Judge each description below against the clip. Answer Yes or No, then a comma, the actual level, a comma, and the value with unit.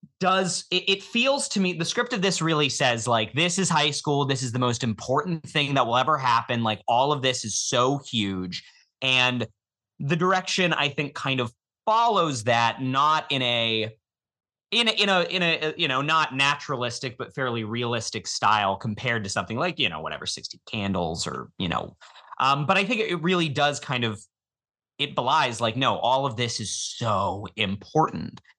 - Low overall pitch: Yes, low, 130 Hz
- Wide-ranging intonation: Yes, wide, 6.2 semitones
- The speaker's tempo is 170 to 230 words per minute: Yes, average, 190 wpm